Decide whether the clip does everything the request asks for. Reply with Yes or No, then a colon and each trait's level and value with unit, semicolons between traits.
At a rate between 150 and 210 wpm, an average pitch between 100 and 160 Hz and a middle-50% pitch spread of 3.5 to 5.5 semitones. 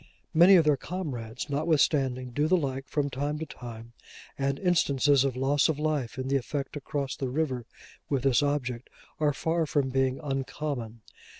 No: average, 175 wpm; medium, 140 Hz; average, 2.7 semitones